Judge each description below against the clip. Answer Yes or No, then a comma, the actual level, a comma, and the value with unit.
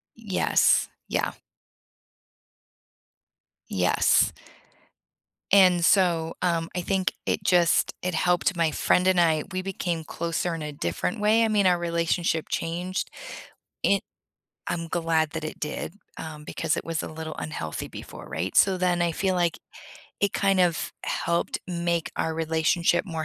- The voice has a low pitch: No, medium, 170 Hz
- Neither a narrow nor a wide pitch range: No, narrow, 2.1 semitones